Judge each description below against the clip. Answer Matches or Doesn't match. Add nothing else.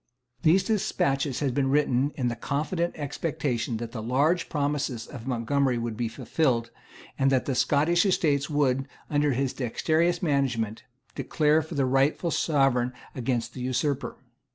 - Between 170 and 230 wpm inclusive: Doesn't match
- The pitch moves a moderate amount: Matches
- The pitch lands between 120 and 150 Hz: Matches